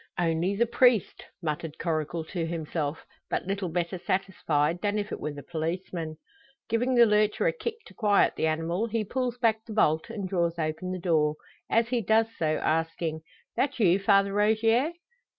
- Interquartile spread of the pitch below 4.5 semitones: No, average, 5.2 semitones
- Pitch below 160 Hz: No, medium, 185 Hz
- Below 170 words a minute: No, average, 175 wpm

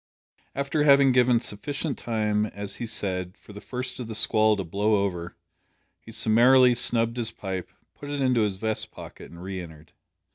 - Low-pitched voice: Yes, low, 110 Hz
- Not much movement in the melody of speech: No, average, 4.1 semitones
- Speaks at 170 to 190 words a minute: Yes, average, 180 wpm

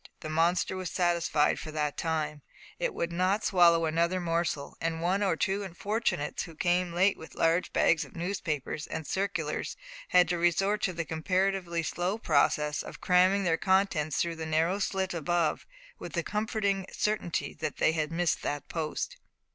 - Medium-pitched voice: Yes, medium, 175 Hz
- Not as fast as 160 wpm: No, average, 170 wpm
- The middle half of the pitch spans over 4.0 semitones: No, average, 3.0 semitones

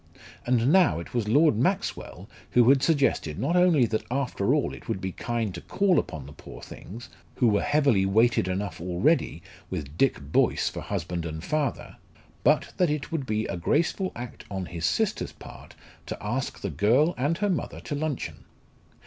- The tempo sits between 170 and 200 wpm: Yes, average, 185 wpm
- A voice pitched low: Yes, low, 120 Hz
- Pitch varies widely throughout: Yes, wide, 7.9 semitones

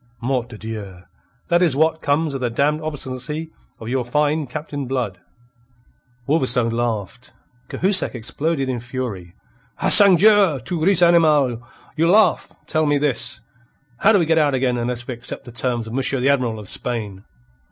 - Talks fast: No, average, 165 wpm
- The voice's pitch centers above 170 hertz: No, low, 135 Hz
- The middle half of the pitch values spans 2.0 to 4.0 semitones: No, average, 4.7 semitones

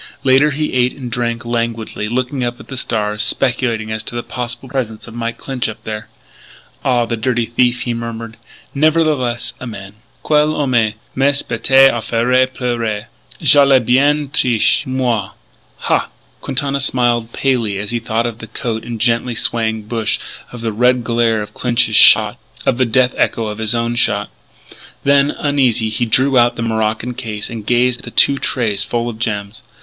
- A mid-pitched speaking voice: No, low, 120 Hz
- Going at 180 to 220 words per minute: Yes, average, 185 wpm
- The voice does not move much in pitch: Yes, narrow, 2.3 semitones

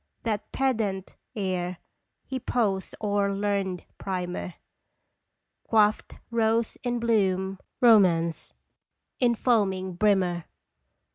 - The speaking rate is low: Yes, slow, 85 wpm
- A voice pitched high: Yes, high, 200 Hz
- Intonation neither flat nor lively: Yes, average, 3.2 semitones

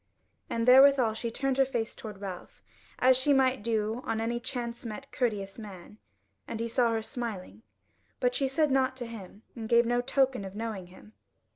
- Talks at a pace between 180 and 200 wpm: Yes, average, 185 wpm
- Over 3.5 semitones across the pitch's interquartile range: No, average, 3.1 semitones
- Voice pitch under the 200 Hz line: No, high, 235 Hz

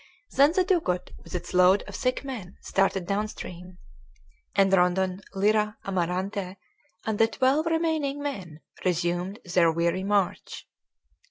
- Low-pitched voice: No, high, 195 Hz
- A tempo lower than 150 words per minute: Yes, slow, 135 wpm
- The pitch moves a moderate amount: Yes, average, 5.0 semitones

